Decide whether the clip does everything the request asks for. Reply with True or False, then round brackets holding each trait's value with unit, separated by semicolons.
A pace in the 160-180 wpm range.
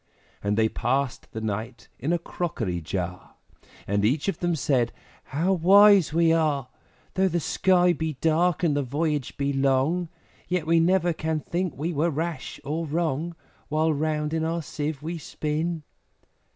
True (165 wpm)